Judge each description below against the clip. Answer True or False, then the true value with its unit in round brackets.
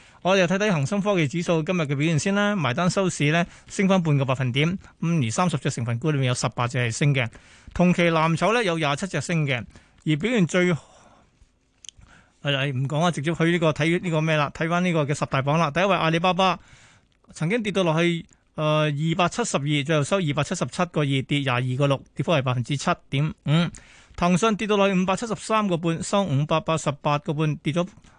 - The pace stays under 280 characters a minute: False (325 characters per minute)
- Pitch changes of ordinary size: True (3.6 semitones)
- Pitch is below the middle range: False (160 Hz)